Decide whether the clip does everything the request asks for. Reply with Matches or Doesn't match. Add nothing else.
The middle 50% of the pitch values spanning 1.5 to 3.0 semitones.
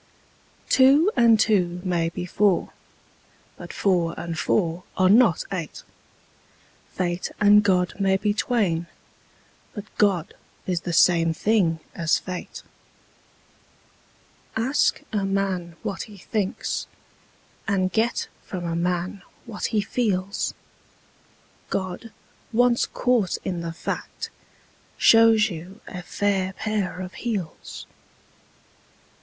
Doesn't match